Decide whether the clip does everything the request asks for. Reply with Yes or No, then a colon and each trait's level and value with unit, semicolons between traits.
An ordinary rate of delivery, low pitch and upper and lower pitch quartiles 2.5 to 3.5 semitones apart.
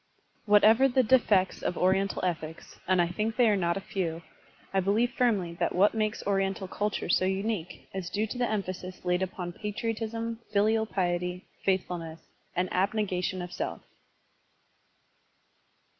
No: average, 160 wpm; high, 195 Hz; average, 3.1 semitones